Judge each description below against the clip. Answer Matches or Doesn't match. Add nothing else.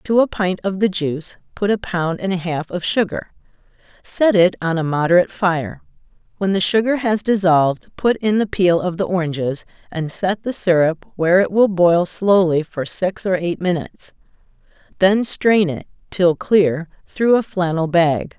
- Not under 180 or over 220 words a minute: Doesn't match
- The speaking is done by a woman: Matches